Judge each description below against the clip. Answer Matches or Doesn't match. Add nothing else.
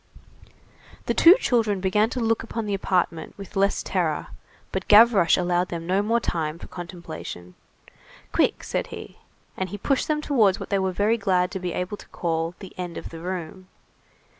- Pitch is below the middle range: Doesn't match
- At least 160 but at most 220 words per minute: Matches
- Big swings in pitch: Doesn't match